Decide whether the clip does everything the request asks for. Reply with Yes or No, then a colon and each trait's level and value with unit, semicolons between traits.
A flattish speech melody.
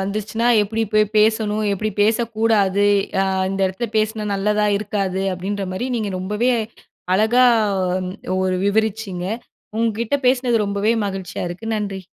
Yes: narrow, 2.2 semitones